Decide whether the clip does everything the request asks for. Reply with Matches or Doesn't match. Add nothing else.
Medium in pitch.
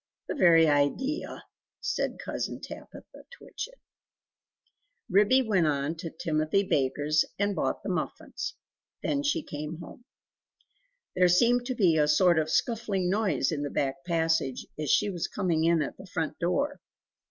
Matches